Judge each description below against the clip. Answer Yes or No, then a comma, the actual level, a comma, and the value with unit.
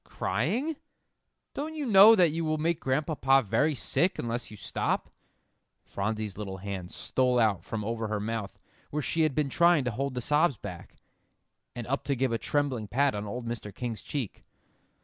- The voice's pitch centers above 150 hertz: No, low, 130 Hz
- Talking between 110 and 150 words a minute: No, average, 180 wpm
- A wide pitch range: Yes, wide, 5.9 semitones